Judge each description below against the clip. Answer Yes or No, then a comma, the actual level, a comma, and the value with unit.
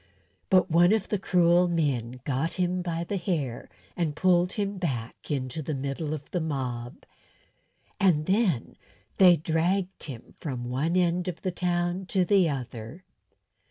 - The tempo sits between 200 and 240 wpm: No, average, 155 wpm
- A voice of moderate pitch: Yes, medium, 170 Hz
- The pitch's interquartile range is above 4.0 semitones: Yes, average, 4.7 semitones